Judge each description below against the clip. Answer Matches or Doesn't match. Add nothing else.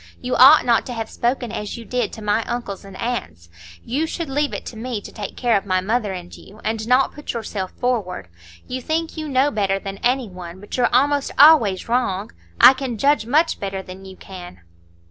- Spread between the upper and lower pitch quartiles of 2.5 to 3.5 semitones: Doesn't match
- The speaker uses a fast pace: Matches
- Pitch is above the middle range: Matches